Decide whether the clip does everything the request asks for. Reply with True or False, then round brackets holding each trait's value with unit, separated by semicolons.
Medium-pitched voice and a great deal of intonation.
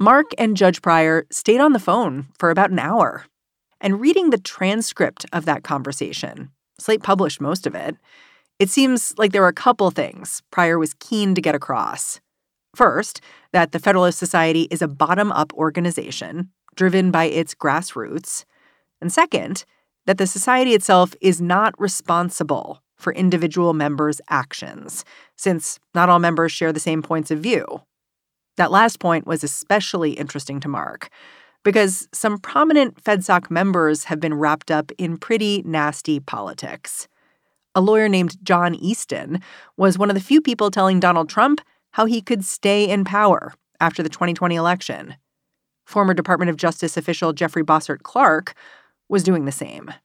False (180 Hz; 4.0 semitones)